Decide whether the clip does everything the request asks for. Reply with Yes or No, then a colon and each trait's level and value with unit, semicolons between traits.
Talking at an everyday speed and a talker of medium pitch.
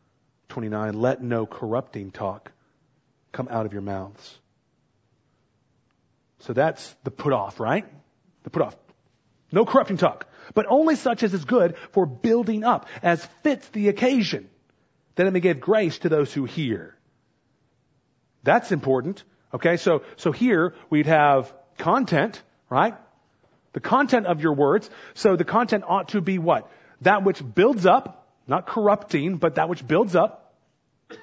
Yes: average, 150 wpm; medium, 165 Hz